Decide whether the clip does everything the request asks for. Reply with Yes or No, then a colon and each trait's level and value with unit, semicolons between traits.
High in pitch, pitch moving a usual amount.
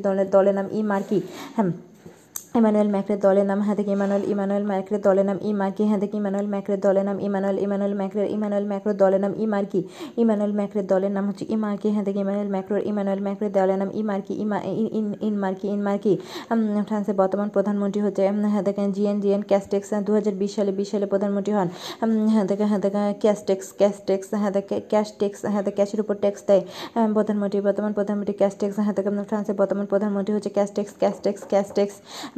No: high, 200 Hz; narrow, 1.0 semitones